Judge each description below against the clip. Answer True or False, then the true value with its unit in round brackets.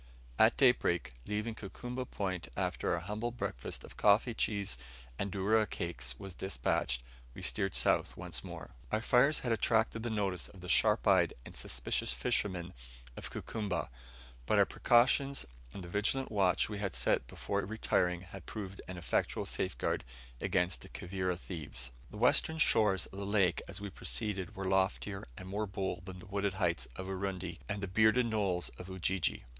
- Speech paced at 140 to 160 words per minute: False (170 wpm)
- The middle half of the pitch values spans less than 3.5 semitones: True (3.0 semitones)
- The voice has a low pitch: True (95 Hz)